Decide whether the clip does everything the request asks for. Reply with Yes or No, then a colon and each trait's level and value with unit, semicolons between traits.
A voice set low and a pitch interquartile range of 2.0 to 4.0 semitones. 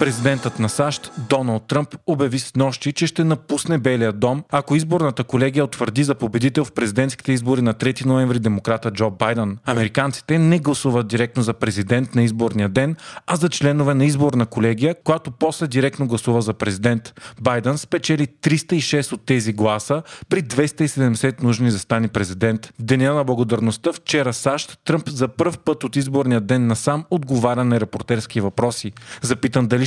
Yes: low, 130 Hz; average, 3.6 semitones